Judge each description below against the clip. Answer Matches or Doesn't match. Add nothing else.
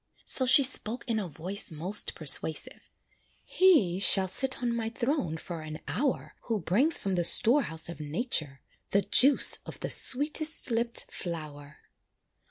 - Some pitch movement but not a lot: Doesn't match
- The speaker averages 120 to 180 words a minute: Matches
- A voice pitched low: Doesn't match